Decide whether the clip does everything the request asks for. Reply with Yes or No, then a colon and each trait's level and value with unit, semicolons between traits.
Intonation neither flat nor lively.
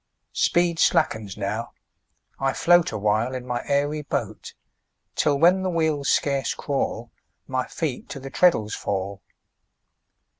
No: wide, 5.9 semitones